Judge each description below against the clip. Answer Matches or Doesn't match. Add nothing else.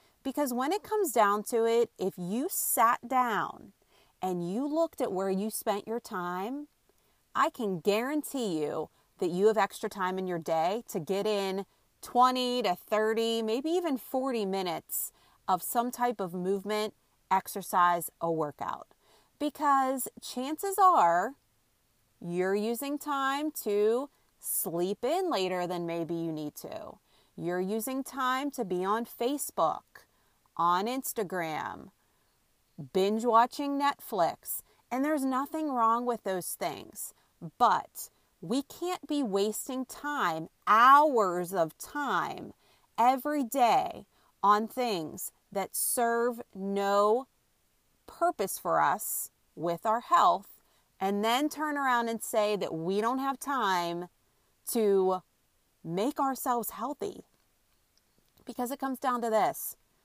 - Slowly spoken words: Matches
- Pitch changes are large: Matches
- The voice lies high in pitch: Matches